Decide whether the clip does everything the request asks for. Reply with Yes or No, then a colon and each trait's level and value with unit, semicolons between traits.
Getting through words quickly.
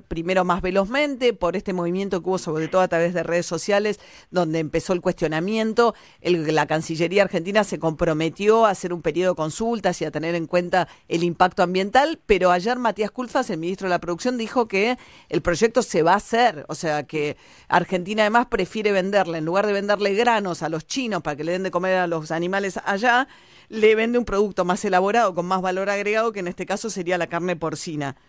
Yes: fast, 210 wpm